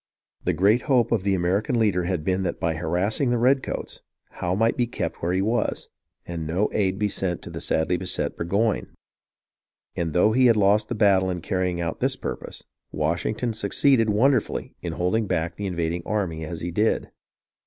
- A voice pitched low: Yes, very low, 95 Hz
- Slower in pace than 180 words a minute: No, average, 185 wpm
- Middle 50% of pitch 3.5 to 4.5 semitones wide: Yes, average, 4.1 semitones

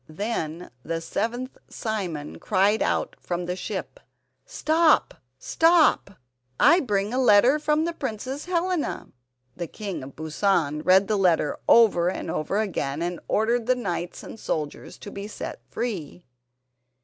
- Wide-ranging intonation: Yes, wide, 6.4 semitones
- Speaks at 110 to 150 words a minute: Yes, average, 140 wpm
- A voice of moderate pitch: No, high, 205 Hz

